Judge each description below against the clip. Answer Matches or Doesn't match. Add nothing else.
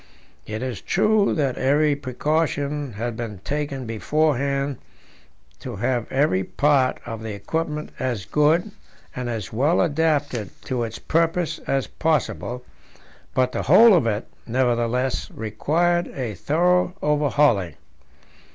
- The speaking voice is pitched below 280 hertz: Matches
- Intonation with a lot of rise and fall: Doesn't match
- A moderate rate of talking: Doesn't match